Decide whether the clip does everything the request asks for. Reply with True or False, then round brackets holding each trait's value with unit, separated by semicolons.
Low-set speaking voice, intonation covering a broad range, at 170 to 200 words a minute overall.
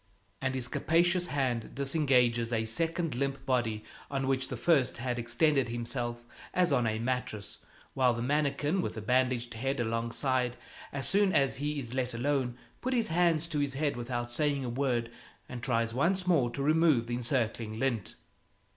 False (130 Hz; 3.4 semitones; 175 wpm)